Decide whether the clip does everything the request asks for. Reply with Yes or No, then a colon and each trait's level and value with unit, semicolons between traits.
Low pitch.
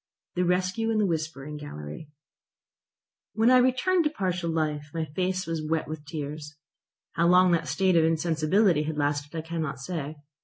No: medium, 165 Hz